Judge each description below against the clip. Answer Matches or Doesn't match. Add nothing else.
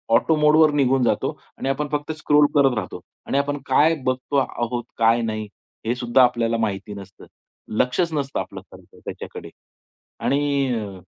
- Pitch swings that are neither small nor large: Matches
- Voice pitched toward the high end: Doesn't match